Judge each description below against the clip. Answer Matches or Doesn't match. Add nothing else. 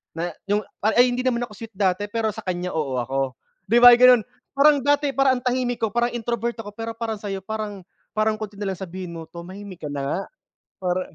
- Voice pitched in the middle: Doesn't match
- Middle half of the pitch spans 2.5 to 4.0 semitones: Doesn't match